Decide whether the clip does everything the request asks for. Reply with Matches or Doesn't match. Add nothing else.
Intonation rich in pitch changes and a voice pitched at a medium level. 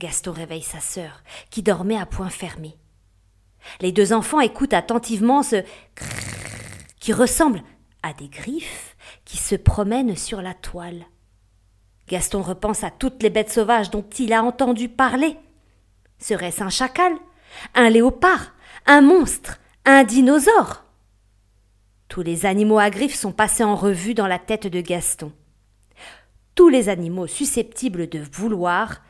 Doesn't match